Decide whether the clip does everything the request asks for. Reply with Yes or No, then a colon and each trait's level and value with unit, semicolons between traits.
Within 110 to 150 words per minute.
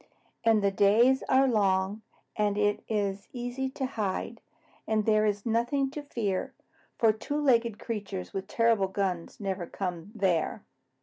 Yes: average, 145 wpm